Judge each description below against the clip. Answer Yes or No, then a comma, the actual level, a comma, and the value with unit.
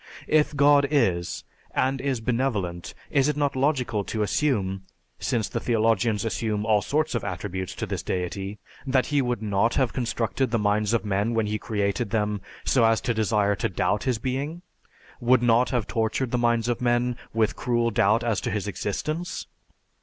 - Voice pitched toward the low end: Yes, low, 115 Hz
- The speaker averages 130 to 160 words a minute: No, average, 180 wpm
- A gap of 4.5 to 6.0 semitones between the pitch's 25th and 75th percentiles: No, average, 3.7 semitones